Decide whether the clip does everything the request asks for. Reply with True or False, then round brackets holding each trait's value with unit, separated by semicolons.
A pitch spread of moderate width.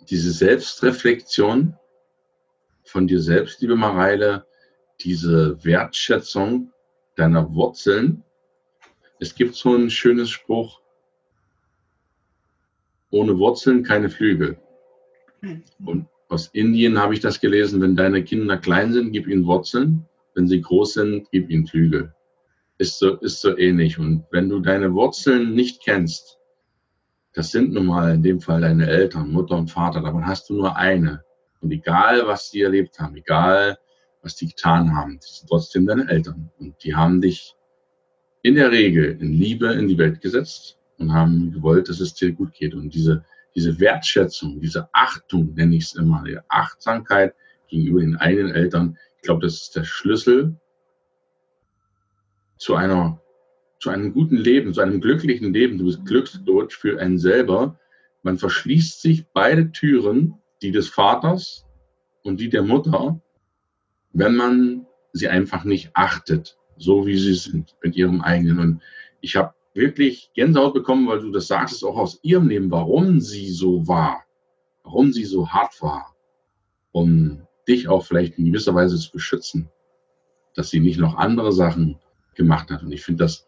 False (6.5 semitones)